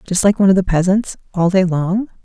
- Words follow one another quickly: Yes, fast, 240 wpm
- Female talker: Yes, female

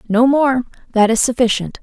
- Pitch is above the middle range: Yes, high, 240 Hz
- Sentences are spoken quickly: No, average, 165 wpm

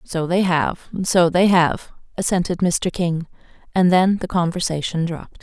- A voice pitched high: No, medium, 175 Hz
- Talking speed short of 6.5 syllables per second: Yes, 4.5 syllables/s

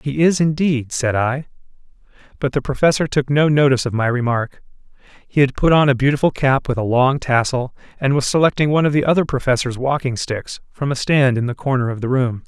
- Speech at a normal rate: No, fast, 210 wpm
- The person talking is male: Yes, male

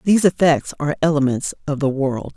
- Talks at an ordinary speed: Yes, average, 180 wpm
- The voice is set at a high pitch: No, medium, 150 Hz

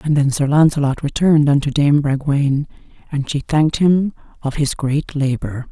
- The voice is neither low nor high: Yes, medium, 145 Hz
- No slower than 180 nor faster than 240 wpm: No, average, 170 wpm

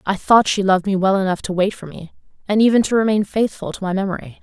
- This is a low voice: No, high, 195 Hz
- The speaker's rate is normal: No, fast, 260 wpm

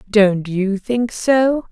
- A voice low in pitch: No, high, 215 Hz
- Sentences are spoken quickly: No, average, 140 wpm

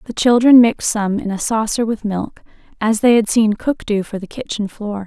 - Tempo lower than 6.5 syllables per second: Yes, 5.1 syllables/s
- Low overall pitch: No, high, 220 Hz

